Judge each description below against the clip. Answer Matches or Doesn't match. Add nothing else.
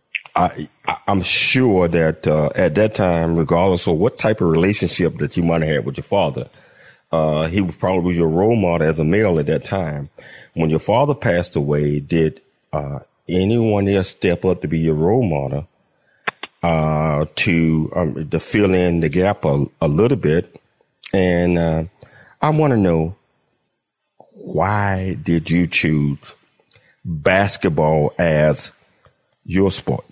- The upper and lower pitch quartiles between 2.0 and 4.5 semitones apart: Matches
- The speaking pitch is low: Matches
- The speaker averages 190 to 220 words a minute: Doesn't match